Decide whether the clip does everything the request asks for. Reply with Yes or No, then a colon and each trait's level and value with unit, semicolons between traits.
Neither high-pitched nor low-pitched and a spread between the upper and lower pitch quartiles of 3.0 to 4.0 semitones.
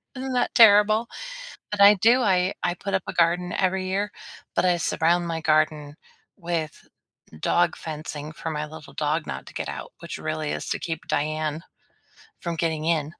Yes: medium, 170 Hz; average, 3.5 semitones